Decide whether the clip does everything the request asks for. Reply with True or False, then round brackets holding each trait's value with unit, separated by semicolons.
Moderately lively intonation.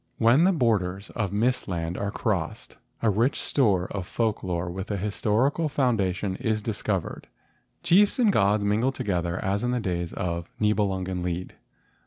True (4.3 semitones)